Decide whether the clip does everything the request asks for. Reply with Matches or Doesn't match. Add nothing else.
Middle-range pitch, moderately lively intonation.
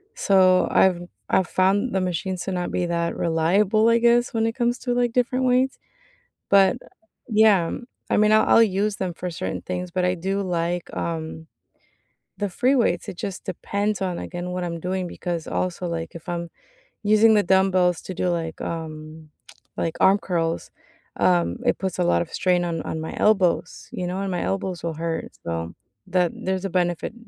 Matches